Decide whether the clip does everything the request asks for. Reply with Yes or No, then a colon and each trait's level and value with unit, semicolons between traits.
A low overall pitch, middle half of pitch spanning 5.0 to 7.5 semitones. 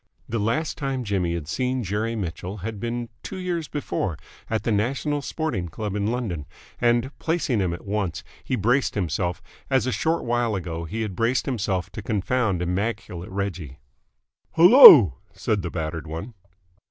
Yes: low, 105 Hz; wide, 5.6 semitones